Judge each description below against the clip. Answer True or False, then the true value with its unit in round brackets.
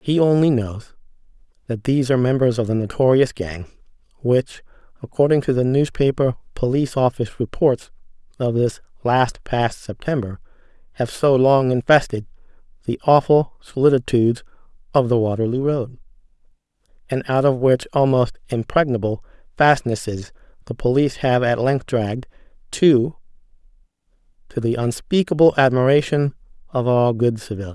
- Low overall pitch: True (125 Hz)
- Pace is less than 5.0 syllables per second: False (5.1 syllables/s)